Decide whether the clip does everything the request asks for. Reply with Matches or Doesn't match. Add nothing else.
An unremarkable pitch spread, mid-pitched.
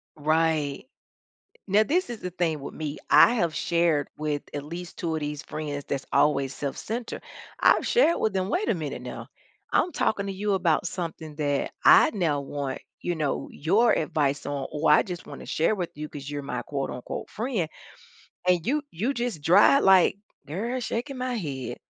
Doesn't match